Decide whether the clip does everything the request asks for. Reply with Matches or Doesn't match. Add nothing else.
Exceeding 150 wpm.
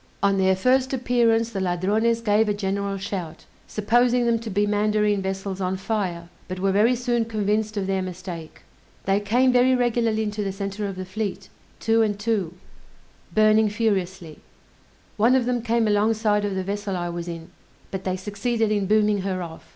Matches